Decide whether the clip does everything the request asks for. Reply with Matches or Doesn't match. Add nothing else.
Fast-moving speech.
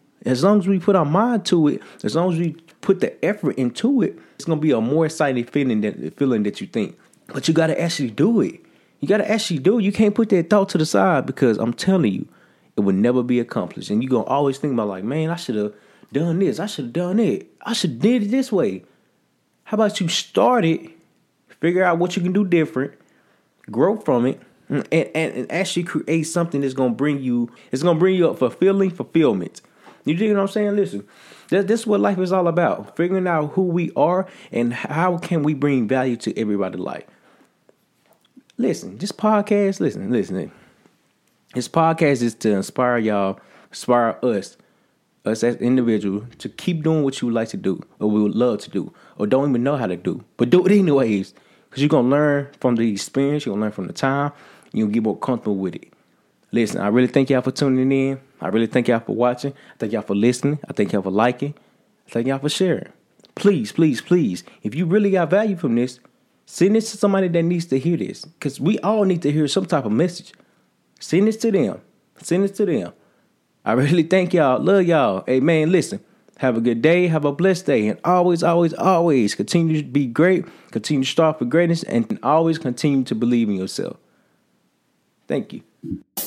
Matches